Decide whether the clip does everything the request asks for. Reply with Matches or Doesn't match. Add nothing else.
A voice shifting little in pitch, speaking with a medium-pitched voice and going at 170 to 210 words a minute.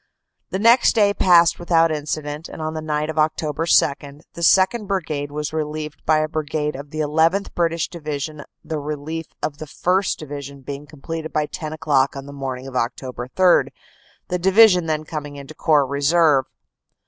Matches